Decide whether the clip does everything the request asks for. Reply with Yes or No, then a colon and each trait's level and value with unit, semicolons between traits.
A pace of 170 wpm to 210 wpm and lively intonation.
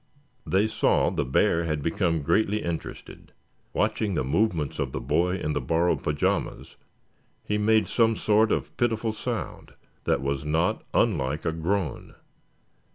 No: average, 145 wpm; wide, 6.0 semitones